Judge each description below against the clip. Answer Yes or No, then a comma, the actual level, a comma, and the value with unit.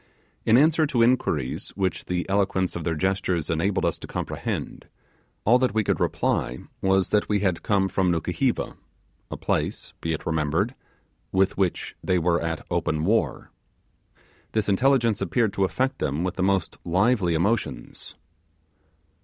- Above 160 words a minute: No, average, 155 wpm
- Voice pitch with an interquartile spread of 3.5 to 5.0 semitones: Yes, average, 4.3 semitones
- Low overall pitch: Yes, very low, 95 Hz